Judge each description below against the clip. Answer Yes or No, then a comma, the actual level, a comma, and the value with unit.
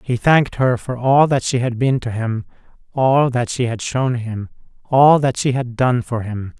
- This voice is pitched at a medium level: No, low, 125 Hz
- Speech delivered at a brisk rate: Yes, fast, 220 wpm